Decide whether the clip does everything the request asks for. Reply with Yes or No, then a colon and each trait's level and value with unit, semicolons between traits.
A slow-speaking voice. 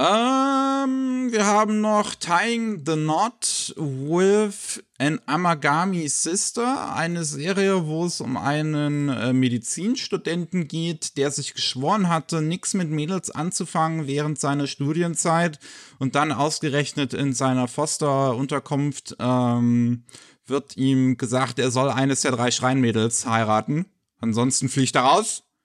Yes: slow, 120 wpm